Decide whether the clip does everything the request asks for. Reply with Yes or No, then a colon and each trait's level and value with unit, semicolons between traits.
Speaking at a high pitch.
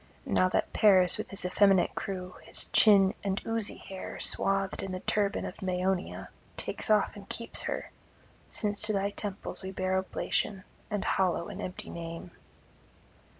Yes: high, 195 Hz